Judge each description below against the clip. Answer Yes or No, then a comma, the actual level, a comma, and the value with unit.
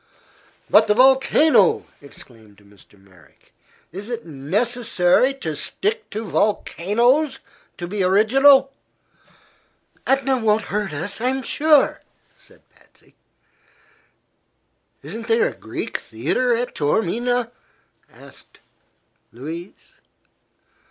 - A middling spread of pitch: No, wide, 7.3 semitones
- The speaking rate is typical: No, slow, 95 wpm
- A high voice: Yes, high, 220 Hz